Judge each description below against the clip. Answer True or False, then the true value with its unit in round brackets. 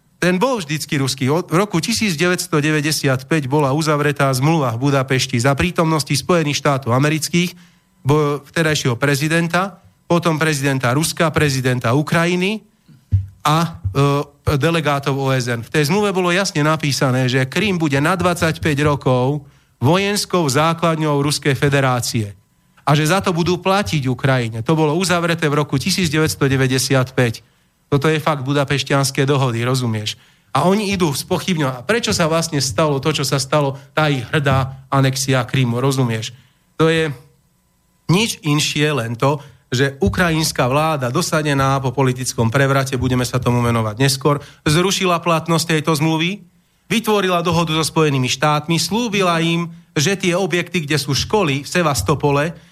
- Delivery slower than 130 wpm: False (135 wpm)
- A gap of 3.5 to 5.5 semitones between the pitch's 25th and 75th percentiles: True (3.8 semitones)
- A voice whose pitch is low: False (150 Hz)